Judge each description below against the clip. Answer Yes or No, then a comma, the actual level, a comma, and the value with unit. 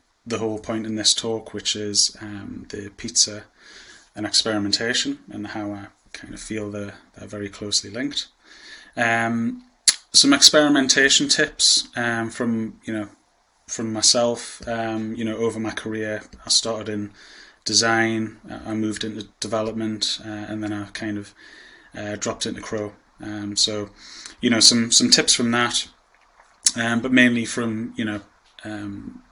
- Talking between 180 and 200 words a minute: No, average, 150 wpm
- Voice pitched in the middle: No, low, 110 Hz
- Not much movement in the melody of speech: Yes, narrow, 1.8 semitones